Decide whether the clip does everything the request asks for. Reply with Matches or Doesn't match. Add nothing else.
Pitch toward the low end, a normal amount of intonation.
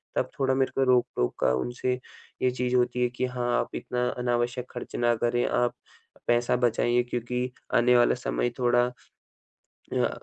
Doesn't match